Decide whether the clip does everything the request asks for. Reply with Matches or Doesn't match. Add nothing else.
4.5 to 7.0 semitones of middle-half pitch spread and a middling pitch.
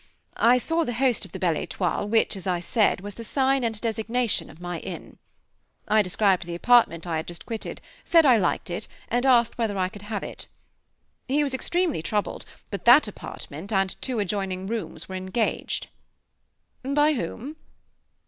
Doesn't match